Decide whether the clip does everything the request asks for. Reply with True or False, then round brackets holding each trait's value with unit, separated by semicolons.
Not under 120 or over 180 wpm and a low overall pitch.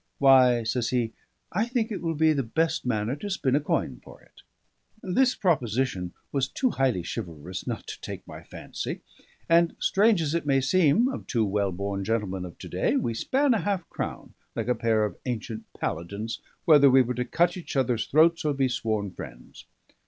False (195 wpm; 130 Hz)